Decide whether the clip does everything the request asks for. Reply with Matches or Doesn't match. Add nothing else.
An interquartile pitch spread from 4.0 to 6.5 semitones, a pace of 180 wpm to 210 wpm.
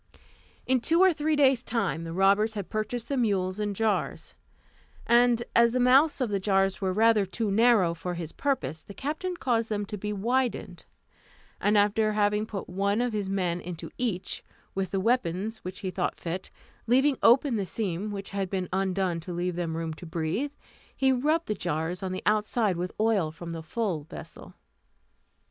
Matches